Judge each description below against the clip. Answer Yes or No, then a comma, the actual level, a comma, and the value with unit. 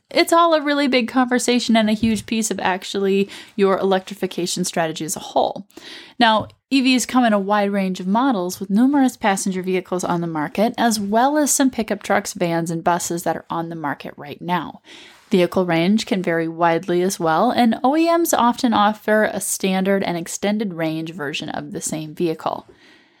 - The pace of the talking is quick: No, average, 185 wpm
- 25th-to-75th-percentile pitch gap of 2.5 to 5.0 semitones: No, wide, 5.6 semitones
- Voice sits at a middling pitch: No, high, 200 Hz